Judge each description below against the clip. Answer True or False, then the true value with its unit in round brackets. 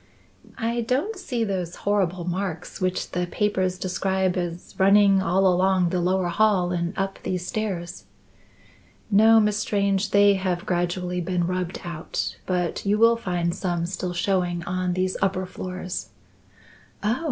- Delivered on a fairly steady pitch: True (2.1 semitones)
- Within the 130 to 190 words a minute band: True (145 wpm)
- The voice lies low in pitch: False (185 Hz)